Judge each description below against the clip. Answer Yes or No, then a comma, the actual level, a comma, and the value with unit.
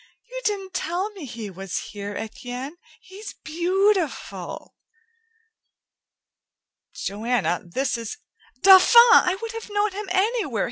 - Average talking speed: No, slow, 120 wpm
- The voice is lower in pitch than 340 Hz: No, very high, 360 Hz